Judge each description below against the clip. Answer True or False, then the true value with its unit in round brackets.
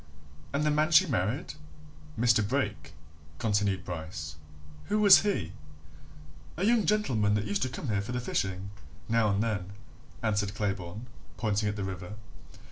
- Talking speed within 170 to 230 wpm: False (150 wpm)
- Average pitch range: True (4.6 semitones)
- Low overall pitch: True (105 Hz)